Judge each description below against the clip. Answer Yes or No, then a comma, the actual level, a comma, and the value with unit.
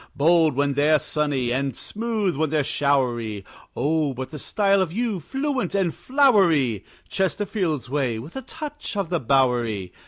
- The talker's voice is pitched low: No, medium, 155 Hz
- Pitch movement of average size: No, wide, 6.9 semitones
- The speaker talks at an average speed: Yes, average, 155 wpm